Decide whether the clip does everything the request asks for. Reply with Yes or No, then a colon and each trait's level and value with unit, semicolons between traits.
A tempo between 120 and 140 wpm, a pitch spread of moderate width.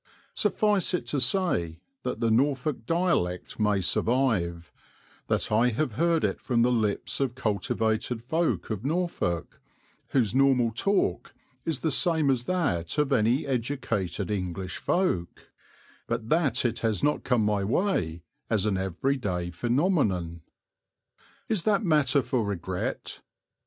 No: slow, 135 wpm; wide, 6.6 semitones